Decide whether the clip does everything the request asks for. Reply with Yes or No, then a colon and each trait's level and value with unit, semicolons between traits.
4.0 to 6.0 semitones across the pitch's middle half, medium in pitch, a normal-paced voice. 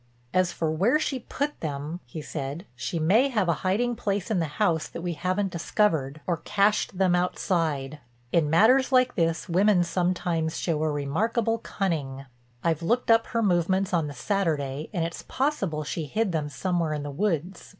Yes: average, 4.8 semitones; medium, 175 Hz; average, 180 wpm